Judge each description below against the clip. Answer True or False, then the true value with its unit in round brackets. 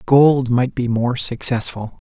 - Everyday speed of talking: True (145 wpm)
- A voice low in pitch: True (125 Hz)